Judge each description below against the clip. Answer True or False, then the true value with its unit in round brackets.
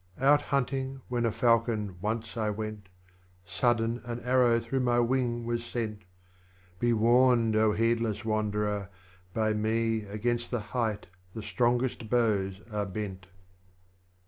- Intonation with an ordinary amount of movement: False (2.2 semitones)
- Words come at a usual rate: False (130 wpm)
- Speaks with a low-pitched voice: True (115 Hz)